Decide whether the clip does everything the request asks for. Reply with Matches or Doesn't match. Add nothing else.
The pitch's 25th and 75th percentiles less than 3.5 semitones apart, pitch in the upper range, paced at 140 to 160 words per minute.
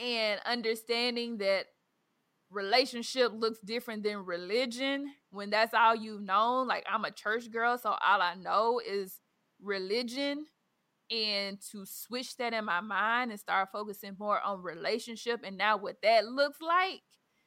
Matches